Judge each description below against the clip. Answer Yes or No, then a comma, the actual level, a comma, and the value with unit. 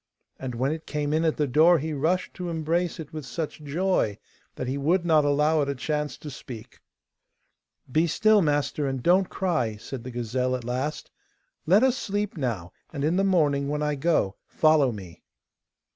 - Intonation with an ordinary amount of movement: Yes, average, 4.1 semitones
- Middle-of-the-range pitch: Yes, medium, 150 Hz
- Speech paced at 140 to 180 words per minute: No, average, 190 wpm